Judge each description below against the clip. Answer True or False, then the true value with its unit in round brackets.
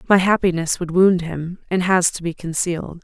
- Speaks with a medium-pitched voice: True (175 Hz)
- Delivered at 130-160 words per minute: False (200 wpm)